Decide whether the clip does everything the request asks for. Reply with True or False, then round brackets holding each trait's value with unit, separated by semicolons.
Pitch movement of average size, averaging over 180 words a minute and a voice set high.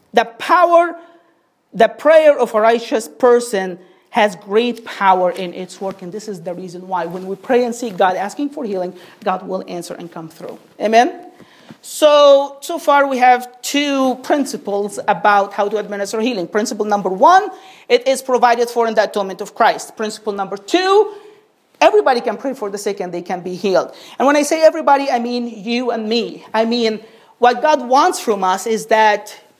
False (5.7 semitones; 190 wpm; 225 Hz)